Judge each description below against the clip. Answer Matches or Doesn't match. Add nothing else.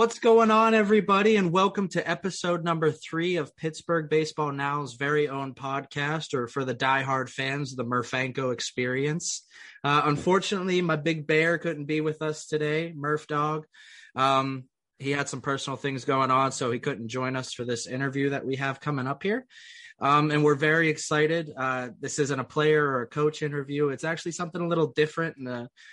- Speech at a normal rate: Matches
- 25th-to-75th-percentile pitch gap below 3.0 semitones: Doesn't match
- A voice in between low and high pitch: Matches